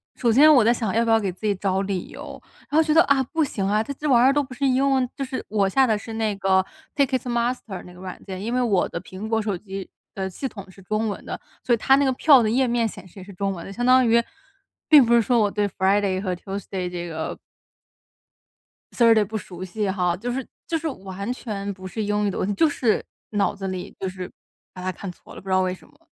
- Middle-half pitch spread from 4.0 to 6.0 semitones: Yes, average, 4.5 semitones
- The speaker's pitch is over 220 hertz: No, high, 210 Hz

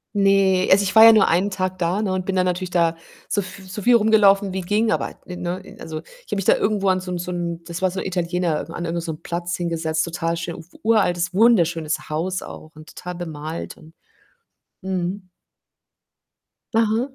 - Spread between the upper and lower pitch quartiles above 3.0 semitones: No, narrow, 2.6 semitones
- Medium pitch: Yes, medium, 180 Hz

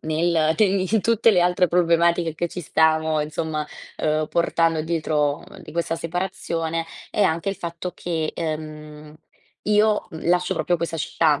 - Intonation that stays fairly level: Yes, narrow, 2.1 semitones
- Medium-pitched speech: Yes, medium, 165 Hz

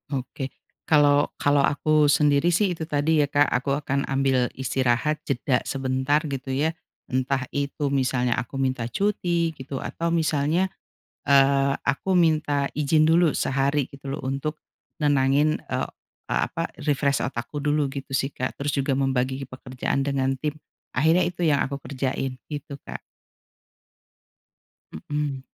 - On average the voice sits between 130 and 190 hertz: Yes, medium, 140 Hz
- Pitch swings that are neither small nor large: No, narrow, 2.2 semitones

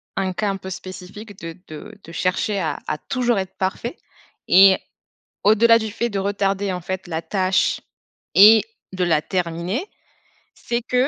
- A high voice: Yes, high, 195 Hz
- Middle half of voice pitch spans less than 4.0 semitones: Yes, average, 2.8 semitones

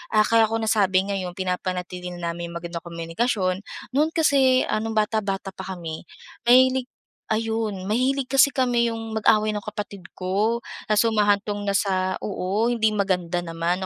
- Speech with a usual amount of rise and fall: Yes, average, 3.6 semitones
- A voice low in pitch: No, high, 205 Hz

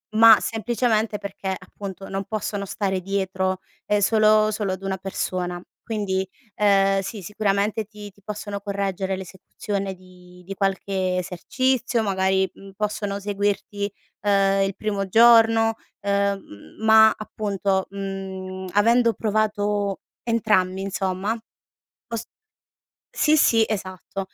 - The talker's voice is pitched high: Yes, high, 200 Hz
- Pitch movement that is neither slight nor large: No, narrow, 2.0 semitones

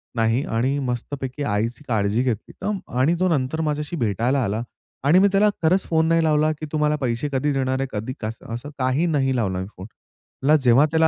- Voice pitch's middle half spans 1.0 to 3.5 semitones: No, average, 4.7 semitones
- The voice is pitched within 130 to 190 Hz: Yes, low, 135 Hz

